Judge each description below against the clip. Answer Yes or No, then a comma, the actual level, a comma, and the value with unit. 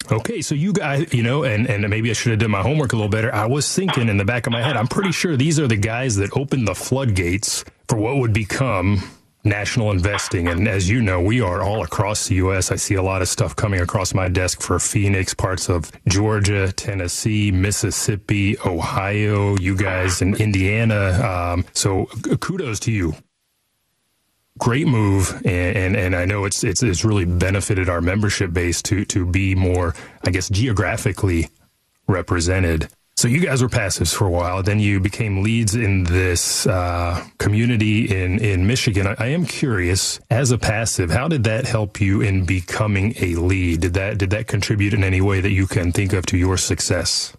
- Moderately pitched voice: No, low, 105 Hz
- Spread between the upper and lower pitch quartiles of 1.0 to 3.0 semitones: No, average, 3.5 semitones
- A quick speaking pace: No, average, 195 wpm